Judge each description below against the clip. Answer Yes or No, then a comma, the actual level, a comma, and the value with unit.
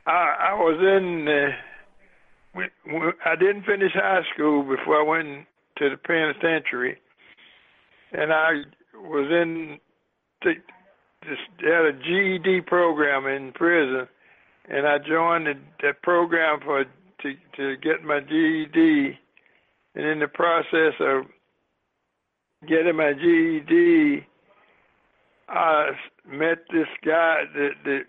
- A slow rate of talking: Yes, slow, 120 wpm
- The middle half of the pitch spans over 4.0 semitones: No, average, 3.4 semitones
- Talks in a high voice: No, medium, 160 Hz